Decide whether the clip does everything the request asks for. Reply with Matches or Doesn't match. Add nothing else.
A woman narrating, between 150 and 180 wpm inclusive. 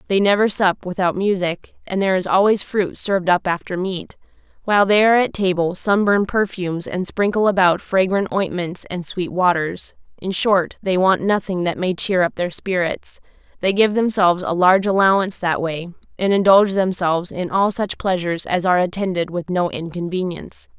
Matches